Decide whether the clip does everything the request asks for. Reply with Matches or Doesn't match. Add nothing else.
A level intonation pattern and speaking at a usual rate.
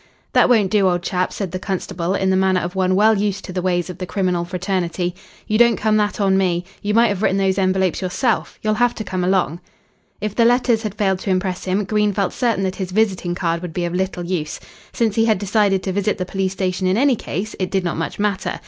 Doesn't match